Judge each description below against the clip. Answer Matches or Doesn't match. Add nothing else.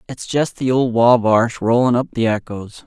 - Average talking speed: Matches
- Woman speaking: Doesn't match